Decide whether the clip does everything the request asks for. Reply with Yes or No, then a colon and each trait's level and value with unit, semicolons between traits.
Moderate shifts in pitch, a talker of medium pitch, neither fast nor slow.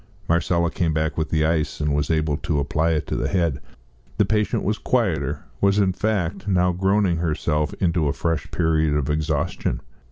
No: average, 3.4 semitones; very low, 80 Hz; average, 185 wpm